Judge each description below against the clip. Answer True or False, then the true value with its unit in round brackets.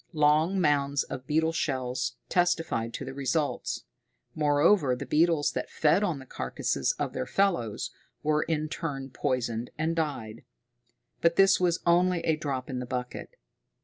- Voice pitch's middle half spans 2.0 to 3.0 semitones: False (4.3 semitones)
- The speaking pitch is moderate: True (150 Hz)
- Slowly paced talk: False (150 wpm)